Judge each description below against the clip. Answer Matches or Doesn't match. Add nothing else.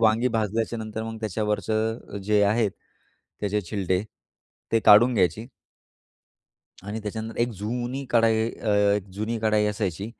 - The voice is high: Doesn't match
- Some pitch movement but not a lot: Doesn't match